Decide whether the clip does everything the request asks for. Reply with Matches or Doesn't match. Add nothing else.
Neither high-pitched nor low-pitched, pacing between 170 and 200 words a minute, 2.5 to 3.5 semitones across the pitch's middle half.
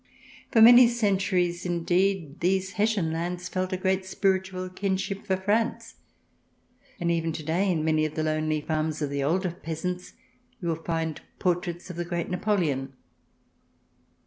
Doesn't match